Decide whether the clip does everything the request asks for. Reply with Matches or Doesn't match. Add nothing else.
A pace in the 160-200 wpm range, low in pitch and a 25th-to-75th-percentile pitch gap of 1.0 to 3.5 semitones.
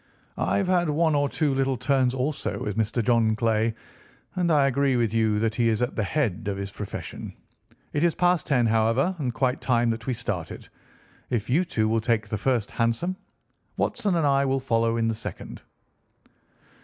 Doesn't match